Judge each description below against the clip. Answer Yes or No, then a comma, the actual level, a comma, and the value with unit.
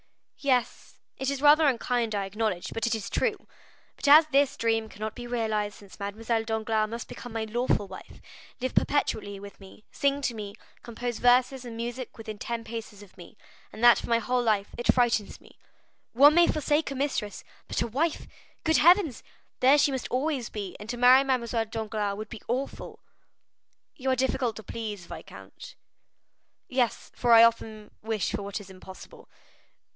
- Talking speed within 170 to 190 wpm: Yes, average, 175 wpm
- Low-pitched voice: No, high, 230 Hz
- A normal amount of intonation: Yes, average, 3.3 semitones